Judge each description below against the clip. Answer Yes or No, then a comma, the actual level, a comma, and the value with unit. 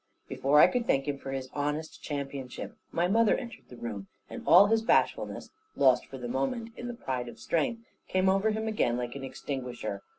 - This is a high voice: No, medium, 140 Hz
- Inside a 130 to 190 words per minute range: No, average, 200 wpm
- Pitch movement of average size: No, wide, 8.6 semitones